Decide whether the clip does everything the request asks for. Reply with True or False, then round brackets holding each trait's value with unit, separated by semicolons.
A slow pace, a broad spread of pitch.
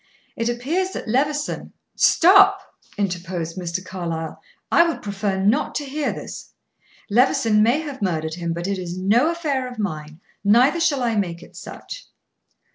False (160 wpm; 8.0 semitones)